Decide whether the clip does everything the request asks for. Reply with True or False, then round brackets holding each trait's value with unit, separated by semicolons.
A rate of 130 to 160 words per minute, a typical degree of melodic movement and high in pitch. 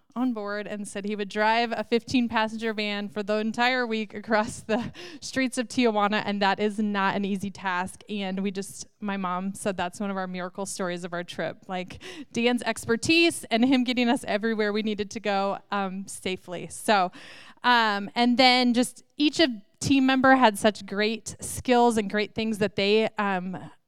False (190 wpm; 3.2 semitones; 215 Hz)